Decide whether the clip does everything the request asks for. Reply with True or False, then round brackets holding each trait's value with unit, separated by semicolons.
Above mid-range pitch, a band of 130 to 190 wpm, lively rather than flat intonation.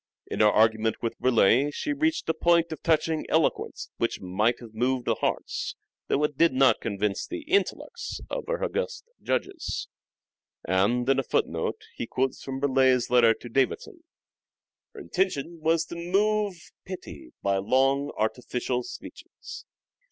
False (135 Hz; 150 wpm; 6.8 semitones)